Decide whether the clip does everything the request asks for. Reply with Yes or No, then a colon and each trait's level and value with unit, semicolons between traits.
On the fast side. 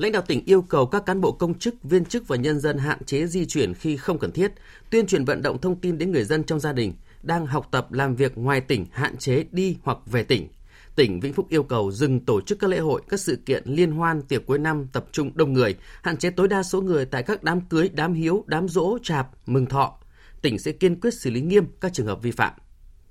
Yes: fast, 260 wpm